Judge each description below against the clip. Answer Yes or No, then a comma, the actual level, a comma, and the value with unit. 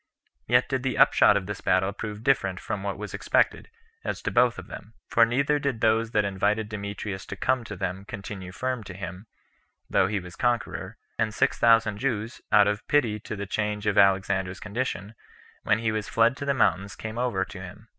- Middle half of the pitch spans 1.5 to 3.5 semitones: Yes, average, 2.7 semitones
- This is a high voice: No, low, 105 Hz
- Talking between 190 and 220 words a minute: Yes, fast, 205 wpm